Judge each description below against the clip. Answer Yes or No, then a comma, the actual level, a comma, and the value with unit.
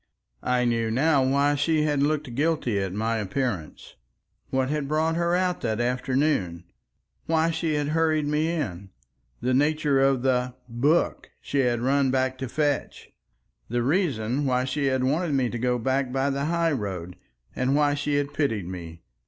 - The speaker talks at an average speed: Yes, average, 170 wpm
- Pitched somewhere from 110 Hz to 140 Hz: Yes, low, 135 Hz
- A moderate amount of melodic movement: Yes, average, 3.7 semitones